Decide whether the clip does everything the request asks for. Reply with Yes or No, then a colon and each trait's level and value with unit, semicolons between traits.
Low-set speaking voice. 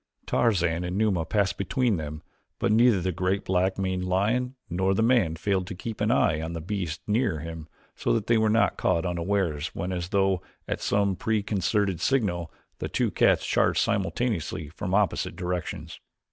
Yes: very low, 95 Hz